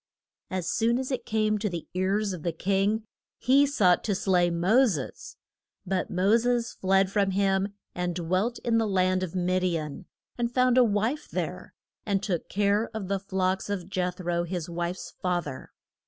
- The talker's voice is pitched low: No, high, 190 Hz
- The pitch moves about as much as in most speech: Yes, average, 3.1 semitones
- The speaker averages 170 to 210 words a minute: Yes, average, 185 wpm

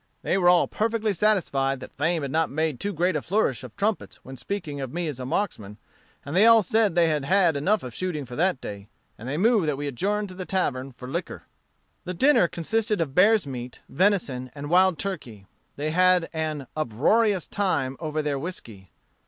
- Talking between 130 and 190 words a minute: No, average, 200 wpm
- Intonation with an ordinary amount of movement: No, wide, 6.1 semitones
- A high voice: No, medium, 165 Hz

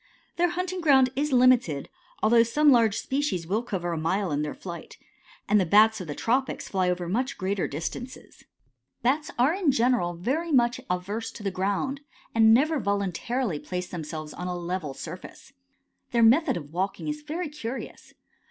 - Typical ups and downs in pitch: No, wide, 6.7 semitones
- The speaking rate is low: No, average, 170 wpm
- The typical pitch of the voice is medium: No, high, 220 Hz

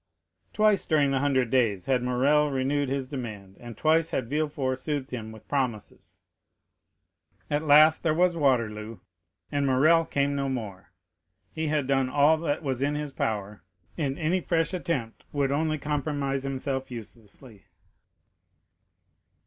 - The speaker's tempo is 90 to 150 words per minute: Yes, average, 140 wpm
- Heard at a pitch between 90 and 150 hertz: Yes, medium, 140 Hz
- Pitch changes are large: No, average, 3.2 semitones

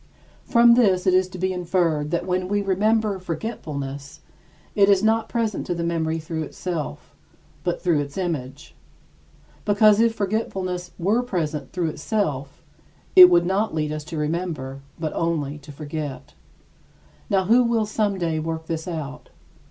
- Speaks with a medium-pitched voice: Yes, medium, 175 Hz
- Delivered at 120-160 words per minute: Yes, average, 150 wpm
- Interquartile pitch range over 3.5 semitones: Yes, average, 4.6 semitones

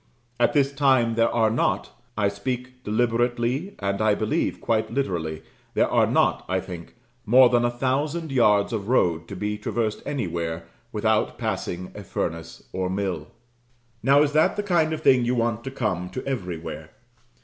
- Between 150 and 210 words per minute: Yes, average, 170 wpm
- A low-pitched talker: Yes, low, 115 Hz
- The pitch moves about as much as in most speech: Yes, average, 4.8 semitones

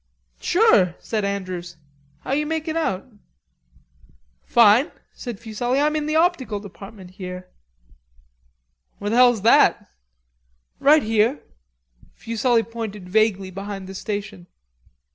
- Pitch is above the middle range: Yes, high, 215 Hz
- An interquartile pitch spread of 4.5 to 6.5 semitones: Yes, average, 4.9 semitones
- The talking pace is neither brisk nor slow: No, slow, 115 wpm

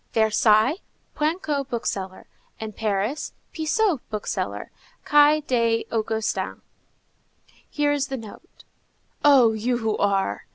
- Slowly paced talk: Yes, slow, 110 wpm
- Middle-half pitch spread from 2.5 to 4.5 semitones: No, average, 5.2 semitones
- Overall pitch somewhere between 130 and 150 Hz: No, high, 235 Hz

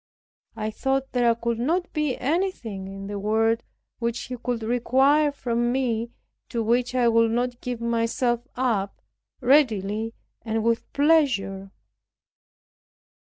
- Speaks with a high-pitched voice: Yes, high, 235 Hz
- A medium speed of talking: No, slow, 125 wpm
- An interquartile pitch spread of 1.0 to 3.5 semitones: Yes, narrow, 2.4 semitones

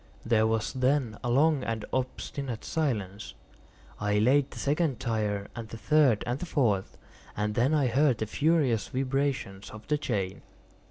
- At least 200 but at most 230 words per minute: No, average, 160 wpm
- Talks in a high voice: No, low, 120 Hz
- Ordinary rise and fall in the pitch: Yes, average, 4.7 semitones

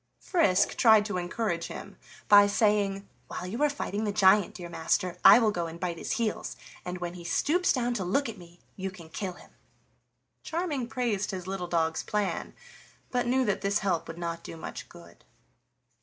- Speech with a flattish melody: No, average, 4.1 semitones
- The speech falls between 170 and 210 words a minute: Yes, average, 190 wpm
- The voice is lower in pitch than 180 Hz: No, high, 195 Hz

